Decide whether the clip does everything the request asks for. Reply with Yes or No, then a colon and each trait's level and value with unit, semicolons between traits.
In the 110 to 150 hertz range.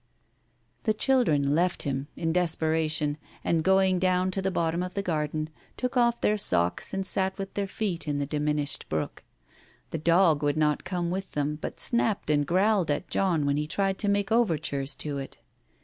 No: medium, 170 Hz